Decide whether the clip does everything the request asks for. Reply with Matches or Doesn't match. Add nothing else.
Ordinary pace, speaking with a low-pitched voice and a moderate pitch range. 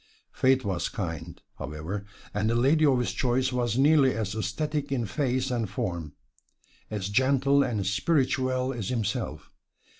Matches